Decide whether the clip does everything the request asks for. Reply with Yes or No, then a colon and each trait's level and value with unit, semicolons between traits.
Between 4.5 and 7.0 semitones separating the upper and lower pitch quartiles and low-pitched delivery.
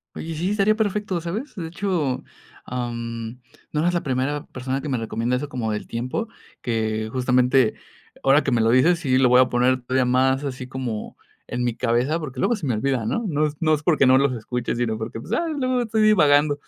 Yes: average, 4.9 semitones; low, 130 Hz